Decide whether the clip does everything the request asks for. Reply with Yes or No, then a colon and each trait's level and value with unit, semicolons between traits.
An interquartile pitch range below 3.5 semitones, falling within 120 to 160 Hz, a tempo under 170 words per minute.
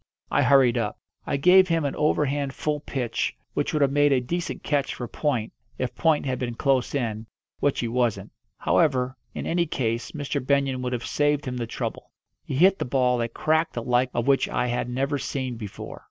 No: average, 3.0 semitones; low, 135 Hz; fast, 205 wpm